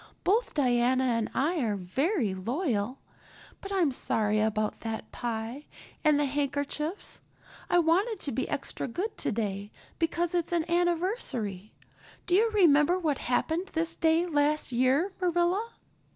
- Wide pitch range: Yes, wide, 6.7 semitones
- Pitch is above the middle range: Yes, very high, 295 Hz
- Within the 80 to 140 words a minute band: Yes, slow, 135 wpm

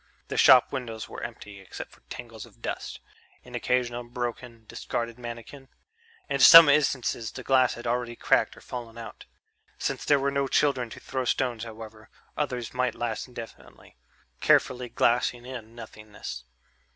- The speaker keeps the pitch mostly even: Yes, narrow, 1.9 semitones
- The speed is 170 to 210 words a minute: No, average, 150 wpm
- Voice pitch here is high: No, low, 120 Hz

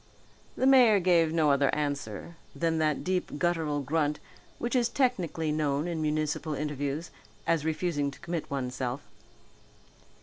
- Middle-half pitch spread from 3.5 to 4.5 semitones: No, average, 3.0 semitones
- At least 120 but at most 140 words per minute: Yes, slow, 135 wpm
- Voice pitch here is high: No, medium, 155 Hz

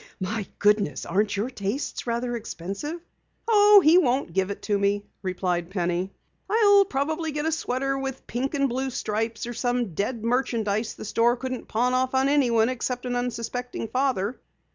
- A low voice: No, high, 245 Hz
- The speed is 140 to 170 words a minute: Yes, average, 165 wpm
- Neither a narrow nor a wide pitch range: Yes, average, 4.5 semitones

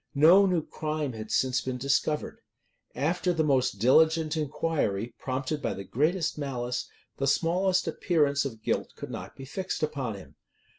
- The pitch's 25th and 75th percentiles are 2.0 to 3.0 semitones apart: No, average, 3.9 semitones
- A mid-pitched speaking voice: Yes, medium, 145 Hz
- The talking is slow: No, average, 155 wpm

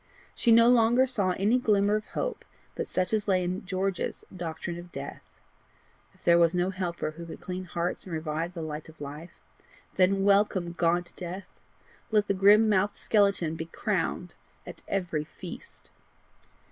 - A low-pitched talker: No, medium, 185 Hz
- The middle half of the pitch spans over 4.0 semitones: No, average, 3.1 semitones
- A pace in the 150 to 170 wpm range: Yes, average, 165 wpm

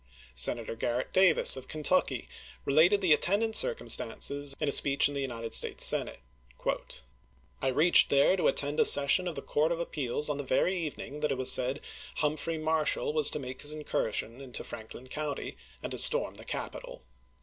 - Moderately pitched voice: Yes, medium, 145 Hz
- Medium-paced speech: Yes, average, 185 wpm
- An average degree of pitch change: Yes, average, 3.6 semitones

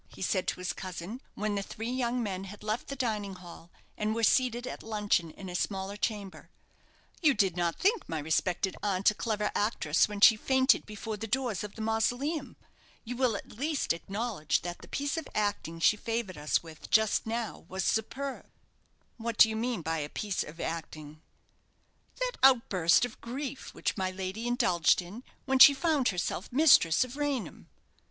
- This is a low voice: No, high, 215 Hz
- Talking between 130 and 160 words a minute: No, average, 185 wpm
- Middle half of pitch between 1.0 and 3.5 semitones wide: No, average, 4.9 semitones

